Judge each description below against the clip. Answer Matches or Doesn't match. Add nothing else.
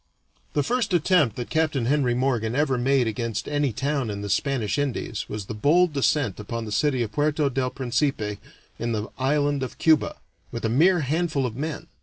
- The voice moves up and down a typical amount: Matches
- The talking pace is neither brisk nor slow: Matches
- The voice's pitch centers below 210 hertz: Matches